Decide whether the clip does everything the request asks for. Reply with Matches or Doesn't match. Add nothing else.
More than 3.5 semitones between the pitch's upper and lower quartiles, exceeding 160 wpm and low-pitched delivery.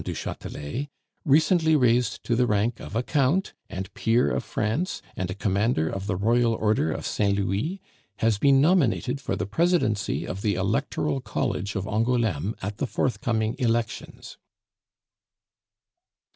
Doesn't match